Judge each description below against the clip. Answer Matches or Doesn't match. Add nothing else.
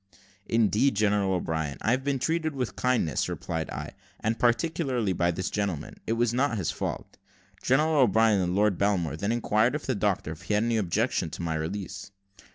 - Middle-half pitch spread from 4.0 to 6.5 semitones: Matches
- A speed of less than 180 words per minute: Doesn't match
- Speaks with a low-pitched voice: Matches